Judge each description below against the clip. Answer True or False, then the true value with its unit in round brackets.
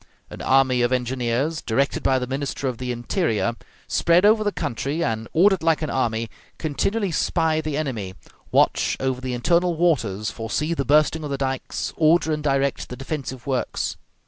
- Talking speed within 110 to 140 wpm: False (170 wpm)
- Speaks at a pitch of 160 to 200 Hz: False (135 Hz)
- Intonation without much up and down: False (4.3 semitones)